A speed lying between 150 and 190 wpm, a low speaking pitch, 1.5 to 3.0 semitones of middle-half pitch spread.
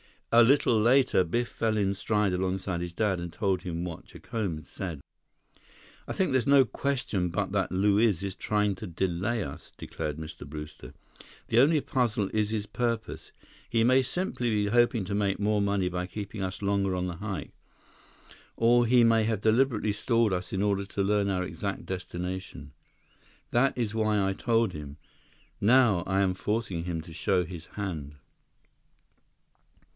No: average, 170 wpm; low, 100 Hz; average, 3.9 semitones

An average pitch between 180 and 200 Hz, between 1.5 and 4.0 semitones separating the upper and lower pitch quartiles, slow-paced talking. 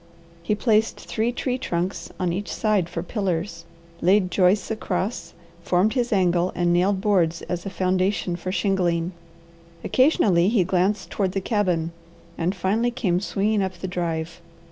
No: medium, 185 Hz; average, 3.0 semitones; average, 150 wpm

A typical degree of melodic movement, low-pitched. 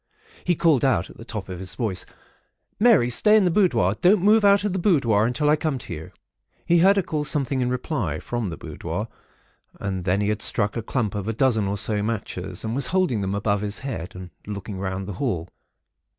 No: wide, 7.5 semitones; low, 115 Hz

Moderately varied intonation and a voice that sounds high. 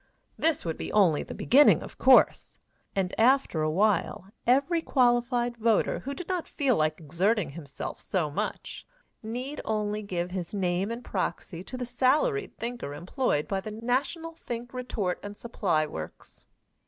No: wide, 5.9 semitones; high, 220 Hz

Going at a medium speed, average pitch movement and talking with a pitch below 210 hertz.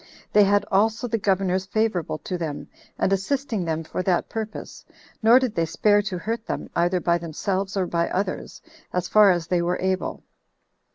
Yes: average, 180 wpm; average, 3.3 semitones; high, 190 Hz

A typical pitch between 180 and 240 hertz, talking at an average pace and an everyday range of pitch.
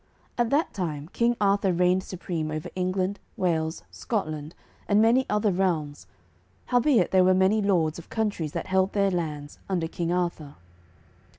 Yes: medium, 185 Hz; average, 155 wpm; average, 3.8 semitones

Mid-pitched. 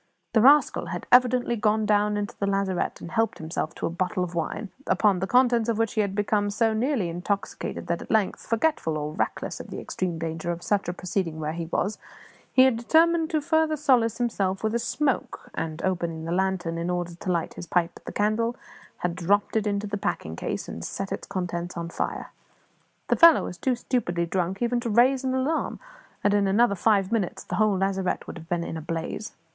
No: high, 200 Hz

